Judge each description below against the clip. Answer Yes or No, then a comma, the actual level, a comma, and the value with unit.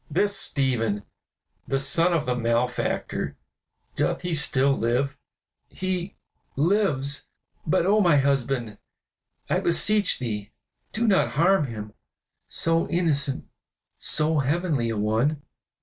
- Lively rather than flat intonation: Yes, wide, 5.8 semitones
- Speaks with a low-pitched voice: No, medium, 145 Hz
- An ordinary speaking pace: No, slow, 115 wpm